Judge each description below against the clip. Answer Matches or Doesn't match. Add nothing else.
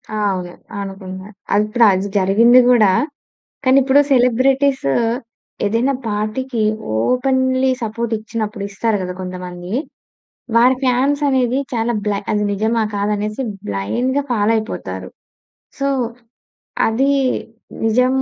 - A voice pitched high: Matches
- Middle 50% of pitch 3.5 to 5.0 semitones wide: Matches